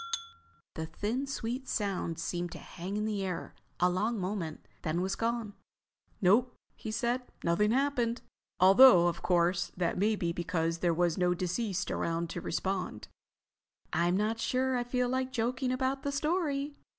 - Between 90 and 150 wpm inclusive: No, average, 160 wpm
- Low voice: No, high, 205 Hz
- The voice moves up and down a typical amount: No, wide, 6.0 semitones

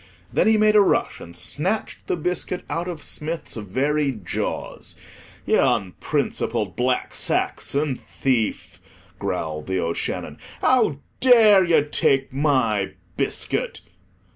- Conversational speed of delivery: No, slow, 115 wpm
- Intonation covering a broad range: Yes, wide, 7.0 semitones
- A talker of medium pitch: Yes, medium, 145 Hz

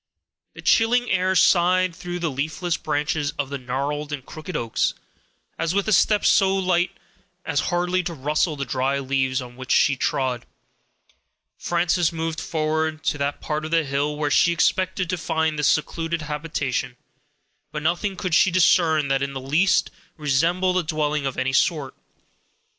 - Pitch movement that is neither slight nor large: Yes, average, 3.8 semitones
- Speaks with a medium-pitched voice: Yes, medium, 155 Hz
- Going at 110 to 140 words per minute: No, average, 165 wpm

